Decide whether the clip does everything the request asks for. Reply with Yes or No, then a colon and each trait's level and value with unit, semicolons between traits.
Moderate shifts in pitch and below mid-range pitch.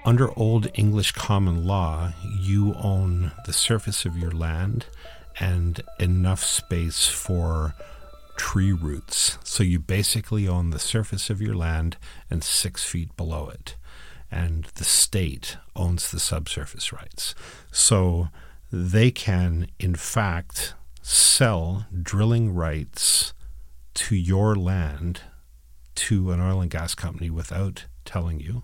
Yes: average, 3.7 semitones; very low, 90 Hz